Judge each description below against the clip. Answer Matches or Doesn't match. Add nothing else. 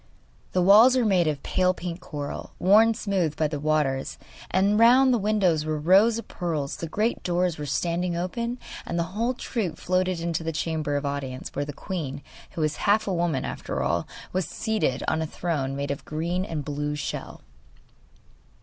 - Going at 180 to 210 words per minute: Matches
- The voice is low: Doesn't match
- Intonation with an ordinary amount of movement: Matches